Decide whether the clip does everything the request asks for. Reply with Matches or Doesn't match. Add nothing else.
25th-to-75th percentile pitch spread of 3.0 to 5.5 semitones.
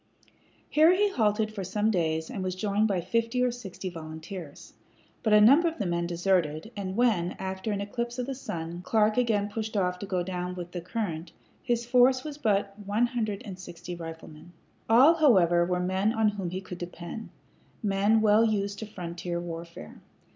Matches